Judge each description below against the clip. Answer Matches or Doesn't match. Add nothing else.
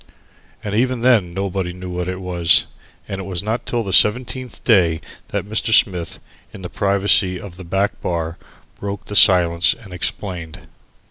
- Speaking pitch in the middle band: Doesn't match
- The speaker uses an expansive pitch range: Doesn't match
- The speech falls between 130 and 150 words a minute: Doesn't match